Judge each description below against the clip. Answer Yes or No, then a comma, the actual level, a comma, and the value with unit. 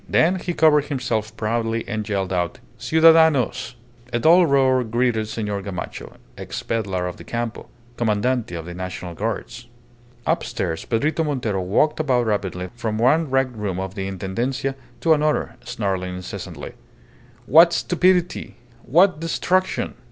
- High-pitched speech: No, low, 115 Hz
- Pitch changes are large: Yes, wide, 7.1 semitones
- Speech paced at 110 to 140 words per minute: Yes, slow, 135 wpm